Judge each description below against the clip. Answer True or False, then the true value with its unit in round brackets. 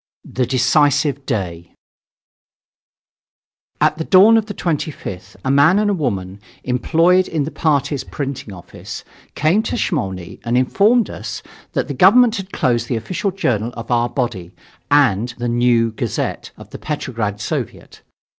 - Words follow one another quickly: False (145 wpm)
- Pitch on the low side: True (130 Hz)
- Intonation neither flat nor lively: False (6.2 semitones)